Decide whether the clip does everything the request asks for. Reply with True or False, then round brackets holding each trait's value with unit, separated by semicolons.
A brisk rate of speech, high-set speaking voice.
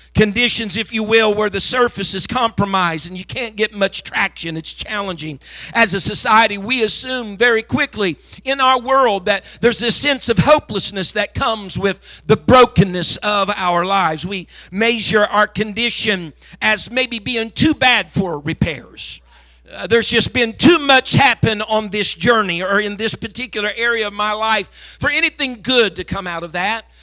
False (175 wpm; 215 Hz)